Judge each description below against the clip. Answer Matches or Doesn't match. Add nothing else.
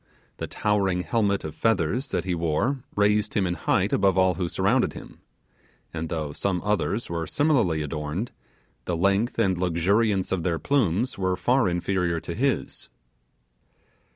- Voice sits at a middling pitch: Doesn't match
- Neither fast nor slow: Matches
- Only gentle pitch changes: Doesn't match